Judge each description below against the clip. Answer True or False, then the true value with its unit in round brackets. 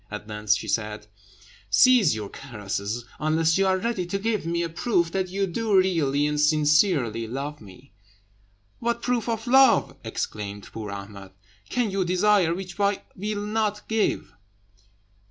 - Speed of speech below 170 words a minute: True (155 wpm)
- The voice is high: False (170 Hz)